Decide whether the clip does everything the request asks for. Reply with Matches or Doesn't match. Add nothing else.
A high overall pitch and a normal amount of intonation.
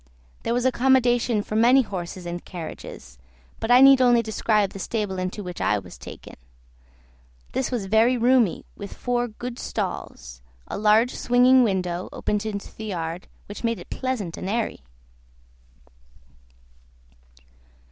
Matches